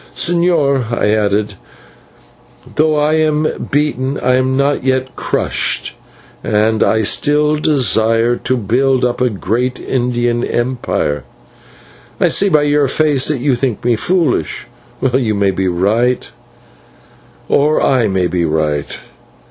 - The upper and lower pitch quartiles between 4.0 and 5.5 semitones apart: Yes, average, 4.9 semitones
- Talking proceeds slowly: Yes, slow, 130 wpm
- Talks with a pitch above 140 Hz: No, low, 125 Hz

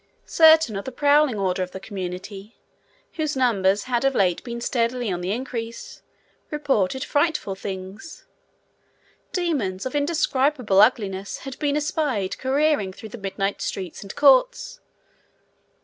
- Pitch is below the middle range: No, high, 235 Hz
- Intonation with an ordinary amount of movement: No, wide, 6.7 semitones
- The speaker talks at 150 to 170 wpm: No, slow, 135 wpm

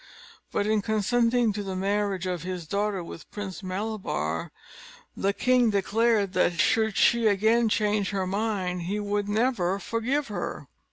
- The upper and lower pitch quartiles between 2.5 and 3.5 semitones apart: Yes, average, 2.8 semitones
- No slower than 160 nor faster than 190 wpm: No, average, 150 wpm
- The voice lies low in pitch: No, high, 205 Hz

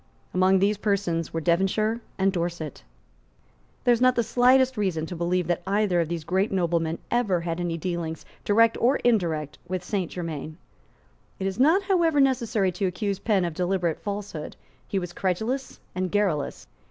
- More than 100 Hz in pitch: Yes, medium, 185 Hz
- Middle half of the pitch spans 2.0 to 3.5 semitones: No, average, 4.0 semitones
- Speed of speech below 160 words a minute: No, average, 165 wpm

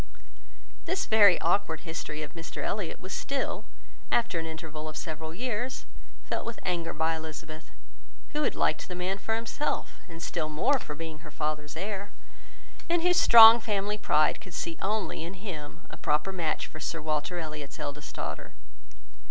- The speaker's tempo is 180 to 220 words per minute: No, average, 170 wpm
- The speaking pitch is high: No, medium, 165 Hz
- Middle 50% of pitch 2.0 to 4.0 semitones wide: No, average, 5.0 semitones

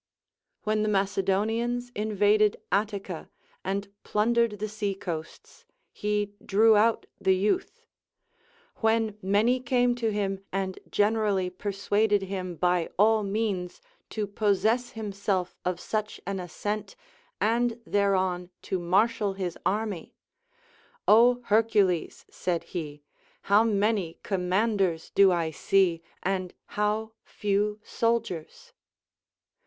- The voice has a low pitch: No, high, 205 Hz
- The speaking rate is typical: No, slow, 105 wpm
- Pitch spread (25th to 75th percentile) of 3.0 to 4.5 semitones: No, narrow, 2.5 semitones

